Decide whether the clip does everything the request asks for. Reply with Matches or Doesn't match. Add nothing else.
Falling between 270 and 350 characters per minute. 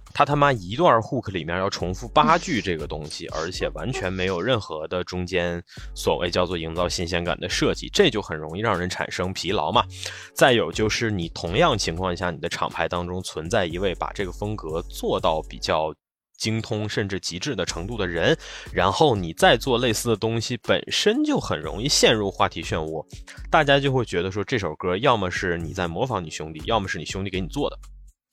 Matches